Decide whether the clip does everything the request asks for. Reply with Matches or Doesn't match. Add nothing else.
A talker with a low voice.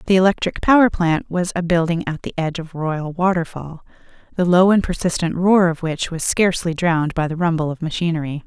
Doesn't match